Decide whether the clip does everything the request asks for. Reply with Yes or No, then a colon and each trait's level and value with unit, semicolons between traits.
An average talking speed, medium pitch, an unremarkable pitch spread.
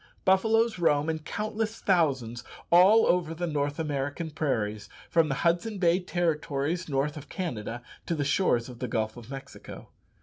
Yes: average, 160 wpm; medium, 155 Hz; average, 4.8 semitones